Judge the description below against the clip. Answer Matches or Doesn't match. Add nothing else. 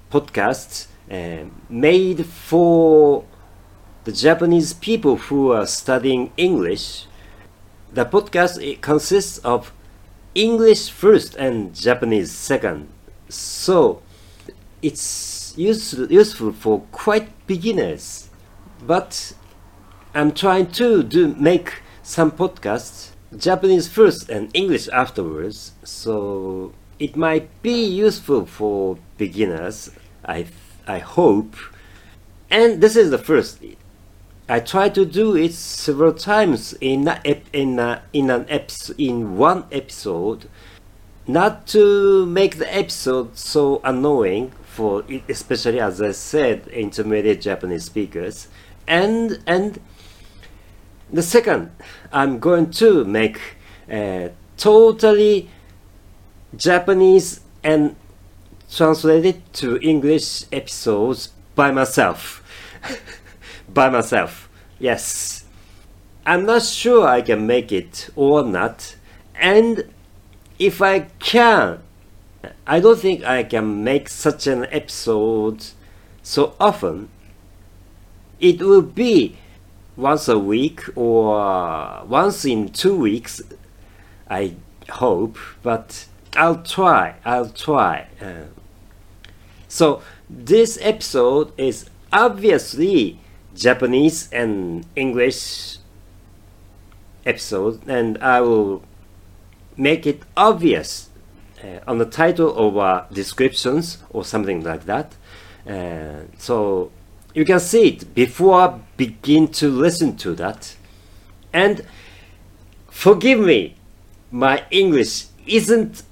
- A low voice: Matches